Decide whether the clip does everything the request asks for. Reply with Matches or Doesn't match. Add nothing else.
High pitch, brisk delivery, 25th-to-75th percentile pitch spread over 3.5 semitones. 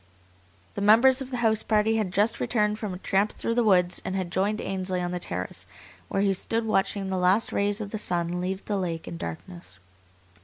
Doesn't match